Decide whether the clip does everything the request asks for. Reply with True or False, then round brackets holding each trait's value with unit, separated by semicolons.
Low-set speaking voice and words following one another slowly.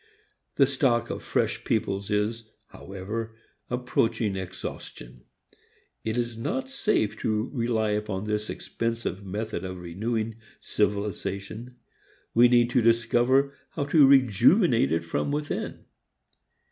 True (115 Hz; 115 wpm)